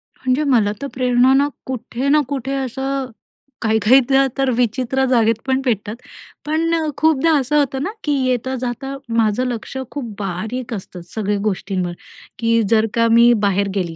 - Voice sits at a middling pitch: No, very high, 250 Hz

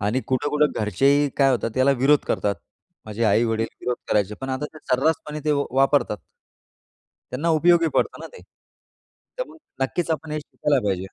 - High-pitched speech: No, low, 135 Hz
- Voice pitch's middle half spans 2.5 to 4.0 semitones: No, average, 4.9 semitones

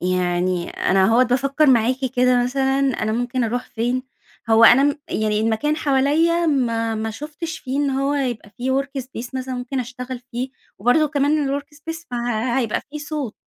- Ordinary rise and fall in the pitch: Yes, average, 3.6 semitones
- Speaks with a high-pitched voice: Yes, very high, 255 Hz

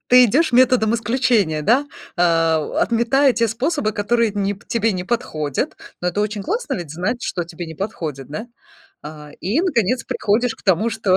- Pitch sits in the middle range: No, high, 215 Hz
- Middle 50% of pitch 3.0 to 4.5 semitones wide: No, wide, 5.5 semitones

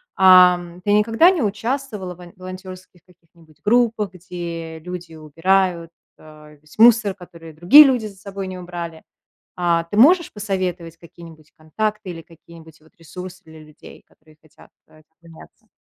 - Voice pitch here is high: No, medium, 180 Hz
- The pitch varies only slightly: No, average, 3.4 semitones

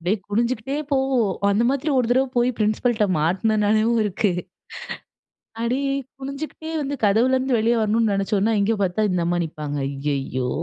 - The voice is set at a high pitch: Yes, high, 220 Hz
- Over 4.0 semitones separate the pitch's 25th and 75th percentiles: Yes, average, 4.7 semitones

